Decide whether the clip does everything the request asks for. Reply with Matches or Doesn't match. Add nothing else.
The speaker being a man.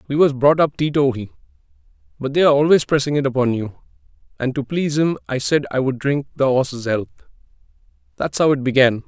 Matches